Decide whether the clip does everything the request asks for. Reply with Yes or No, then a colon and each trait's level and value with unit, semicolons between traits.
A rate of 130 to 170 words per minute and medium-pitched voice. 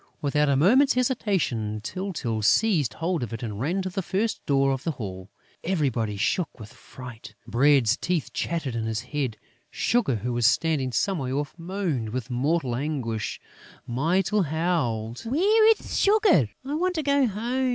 Yes: average, 165 wpm; medium, 145 Hz